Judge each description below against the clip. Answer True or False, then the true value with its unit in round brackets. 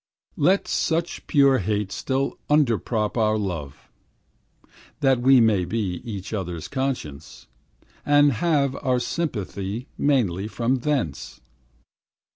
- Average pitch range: False (5.8 semitones)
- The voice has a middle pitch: False (120 Hz)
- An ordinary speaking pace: False (105 wpm)